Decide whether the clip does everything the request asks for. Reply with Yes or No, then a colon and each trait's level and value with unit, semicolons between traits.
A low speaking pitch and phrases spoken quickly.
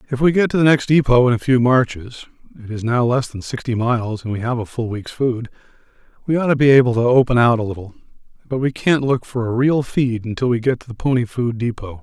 Yes: low, 120 Hz; fast, 255 wpm